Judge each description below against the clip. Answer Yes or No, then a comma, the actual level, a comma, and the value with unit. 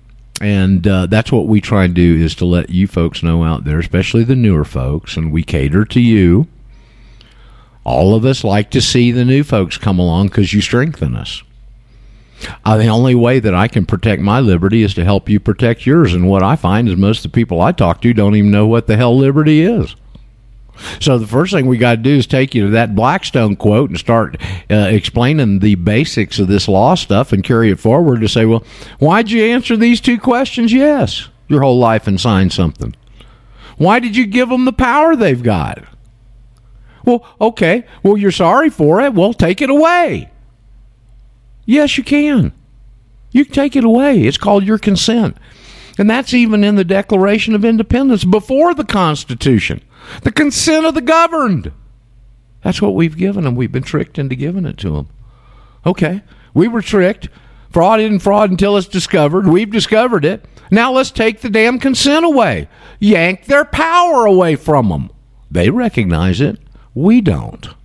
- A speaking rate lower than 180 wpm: No, average, 190 wpm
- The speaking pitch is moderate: No, low, 120 Hz